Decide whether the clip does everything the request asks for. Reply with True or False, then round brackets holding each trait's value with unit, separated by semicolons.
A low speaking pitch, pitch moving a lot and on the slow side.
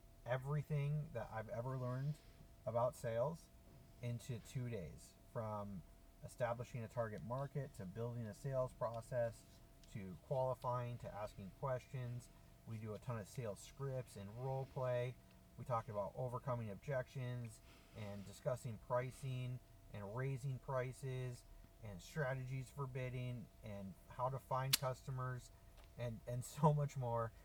False (125 Hz; 2.7 semitones; 130 wpm)